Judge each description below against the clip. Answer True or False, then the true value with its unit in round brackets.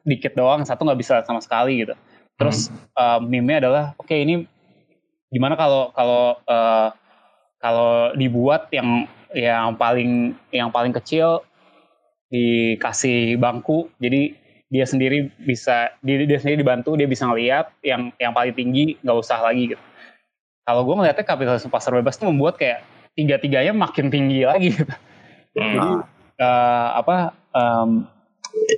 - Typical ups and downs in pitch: True (3.6 semitones)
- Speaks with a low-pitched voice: True (125 Hz)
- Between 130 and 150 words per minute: True (140 wpm)